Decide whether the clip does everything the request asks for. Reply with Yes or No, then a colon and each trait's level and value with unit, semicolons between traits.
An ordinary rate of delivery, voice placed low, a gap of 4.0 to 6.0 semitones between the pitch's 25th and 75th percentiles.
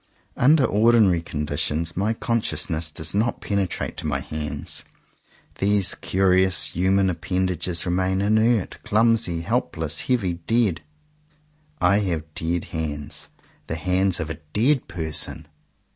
No: slow, 125 wpm; very low, 95 Hz; average, 4.3 semitones